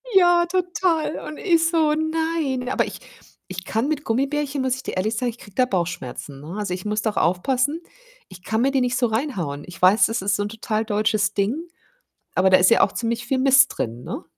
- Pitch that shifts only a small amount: No, wide, 6.9 semitones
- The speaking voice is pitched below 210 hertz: No, high, 235 Hz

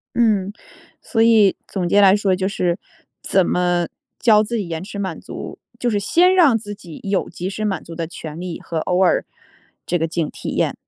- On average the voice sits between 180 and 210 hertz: Yes, high, 190 Hz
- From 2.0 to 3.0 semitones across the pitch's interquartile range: No, average, 3.4 semitones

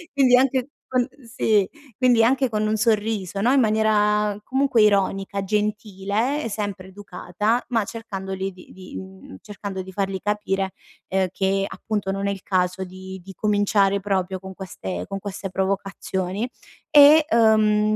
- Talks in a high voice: Yes, high, 205 Hz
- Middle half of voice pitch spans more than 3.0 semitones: No, narrow, 2.4 semitones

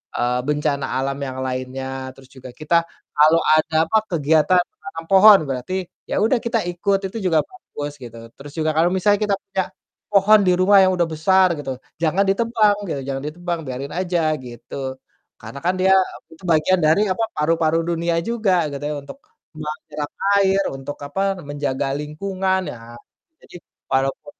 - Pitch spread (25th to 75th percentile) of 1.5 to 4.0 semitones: No, average, 5.0 semitones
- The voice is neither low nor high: Yes, medium, 160 Hz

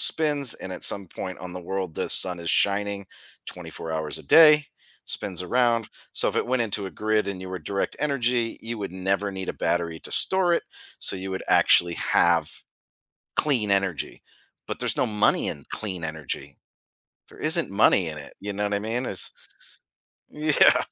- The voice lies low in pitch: Yes, low, 100 Hz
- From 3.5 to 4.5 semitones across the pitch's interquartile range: Yes, average, 4.2 semitones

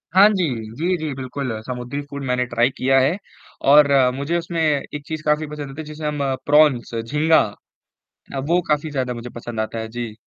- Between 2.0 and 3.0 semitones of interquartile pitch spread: No, average, 3.6 semitones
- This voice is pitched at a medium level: Yes, medium, 145 Hz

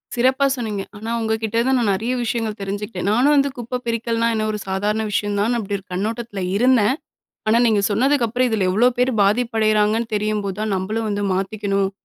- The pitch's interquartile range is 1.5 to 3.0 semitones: Yes, narrow, 2.5 semitones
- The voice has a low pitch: No, high, 220 Hz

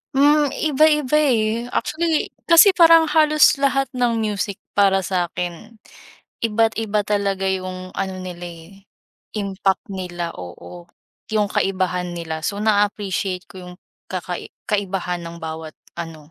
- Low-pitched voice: No, high, 195 Hz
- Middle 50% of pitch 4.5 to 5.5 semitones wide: Yes, average, 4.9 semitones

